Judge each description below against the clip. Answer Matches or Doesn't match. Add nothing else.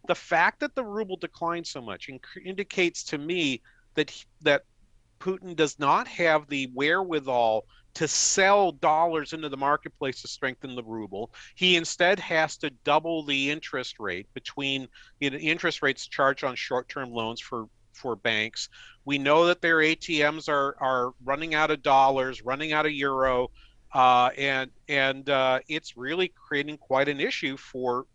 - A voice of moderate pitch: Matches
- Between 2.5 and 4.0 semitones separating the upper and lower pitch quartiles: Matches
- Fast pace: Doesn't match